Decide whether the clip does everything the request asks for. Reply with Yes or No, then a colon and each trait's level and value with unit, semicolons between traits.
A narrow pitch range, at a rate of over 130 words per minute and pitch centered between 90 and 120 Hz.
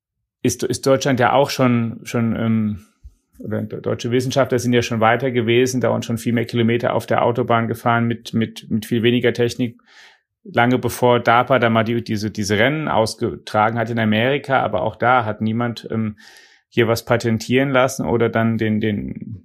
Yes: narrow, 1.6 semitones; average, 180 wpm; low, 115 Hz